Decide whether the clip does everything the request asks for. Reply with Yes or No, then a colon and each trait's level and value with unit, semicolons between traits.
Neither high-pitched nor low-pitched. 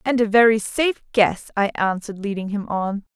No: high, 215 Hz